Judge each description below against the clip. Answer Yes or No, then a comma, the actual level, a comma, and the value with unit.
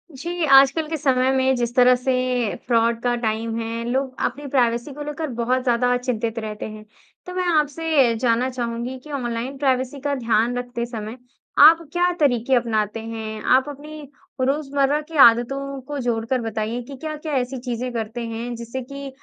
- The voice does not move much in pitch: No, average, 3.1 semitones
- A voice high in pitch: Yes, very high, 250 Hz